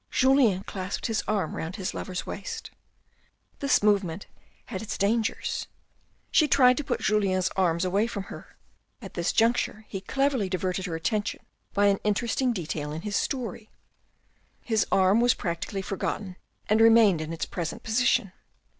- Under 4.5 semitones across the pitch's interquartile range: Yes, average, 3.7 semitones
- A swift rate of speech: No, average, 155 wpm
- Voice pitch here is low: No, high, 205 Hz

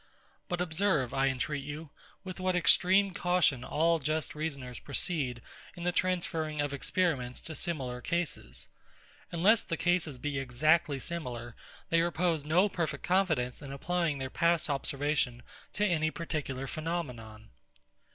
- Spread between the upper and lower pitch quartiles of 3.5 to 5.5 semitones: Yes, average, 4.3 semitones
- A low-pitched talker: No, medium, 155 Hz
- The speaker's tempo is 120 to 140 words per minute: Yes, slow, 135 wpm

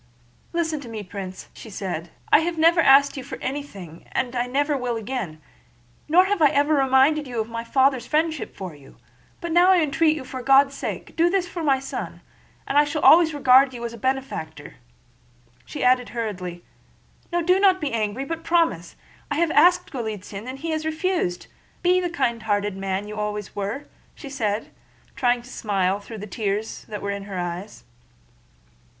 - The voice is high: Yes, very high, 260 Hz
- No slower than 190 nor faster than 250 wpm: No, average, 180 wpm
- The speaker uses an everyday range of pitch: No, wide, 6.9 semitones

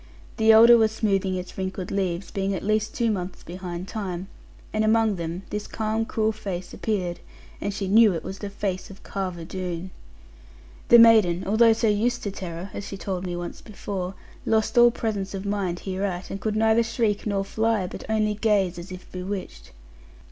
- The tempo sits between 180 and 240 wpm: Yes, average, 185 wpm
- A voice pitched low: No, high, 195 Hz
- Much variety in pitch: No, average, 2.9 semitones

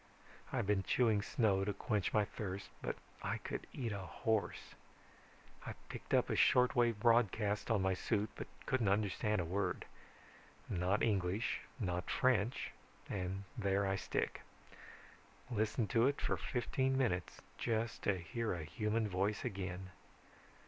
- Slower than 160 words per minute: Yes, average, 145 wpm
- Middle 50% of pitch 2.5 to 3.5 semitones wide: Yes, average, 3.1 semitones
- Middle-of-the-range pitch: No, low, 105 Hz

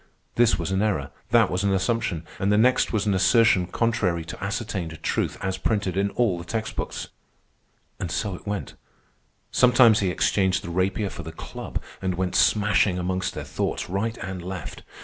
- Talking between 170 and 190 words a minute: Yes, average, 185 wpm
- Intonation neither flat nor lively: Yes, average, 3.1 semitones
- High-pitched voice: No, very low, 95 Hz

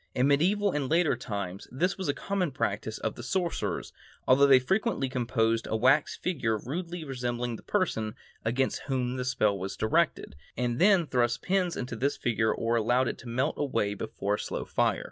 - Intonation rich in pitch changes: Yes, wide, 5.9 semitones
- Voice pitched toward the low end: Yes, low, 130 Hz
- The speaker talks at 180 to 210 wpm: Yes, average, 185 wpm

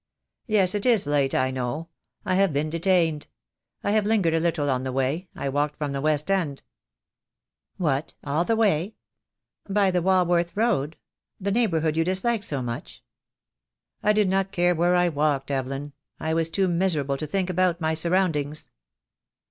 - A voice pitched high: No, medium, 165 Hz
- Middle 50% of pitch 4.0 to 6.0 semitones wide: Yes, average, 4.5 semitones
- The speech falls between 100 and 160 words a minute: No, average, 175 wpm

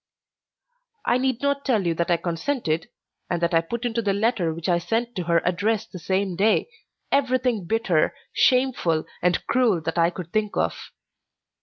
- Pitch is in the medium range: No, high, 200 Hz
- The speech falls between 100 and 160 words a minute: No, average, 175 wpm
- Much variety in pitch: Yes, wide, 5.8 semitones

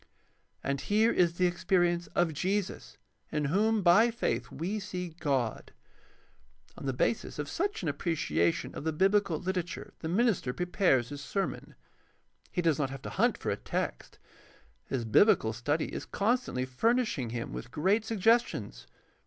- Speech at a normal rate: Yes, average, 155 wpm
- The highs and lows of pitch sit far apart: Yes, wide, 6.5 semitones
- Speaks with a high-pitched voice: No, medium, 175 Hz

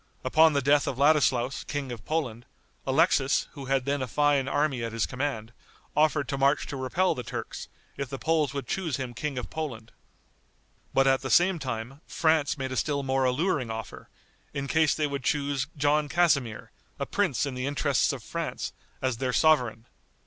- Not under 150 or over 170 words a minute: No, average, 185 wpm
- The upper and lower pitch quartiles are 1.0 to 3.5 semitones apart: Yes, average, 2.9 semitones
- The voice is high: No, medium, 140 Hz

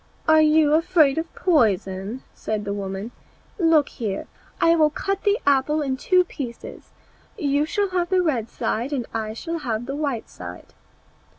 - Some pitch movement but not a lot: No, wide, 6.7 semitones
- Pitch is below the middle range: No, very high, 285 Hz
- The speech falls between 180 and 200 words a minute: No, average, 160 wpm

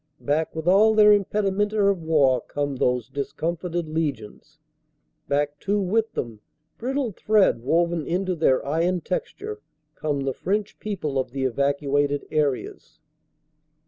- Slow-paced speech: Yes, slow, 130 wpm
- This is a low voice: No, medium, 160 Hz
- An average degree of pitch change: No, wide, 6.0 semitones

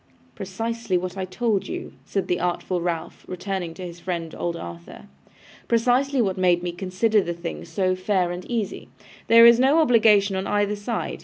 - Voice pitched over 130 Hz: Yes, high, 190 Hz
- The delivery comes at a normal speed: Yes, average, 175 wpm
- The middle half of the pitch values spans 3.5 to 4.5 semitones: Yes, average, 4.2 semitones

